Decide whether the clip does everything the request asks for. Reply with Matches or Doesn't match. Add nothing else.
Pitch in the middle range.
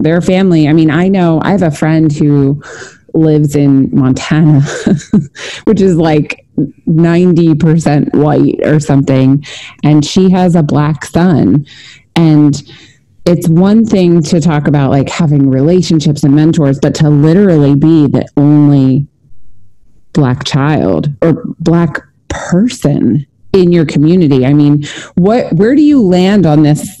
Matches